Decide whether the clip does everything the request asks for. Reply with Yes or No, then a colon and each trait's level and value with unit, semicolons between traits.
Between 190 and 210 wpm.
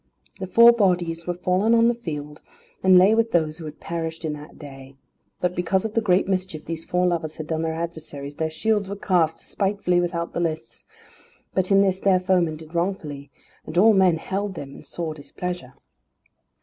Yes: average, 195 wpm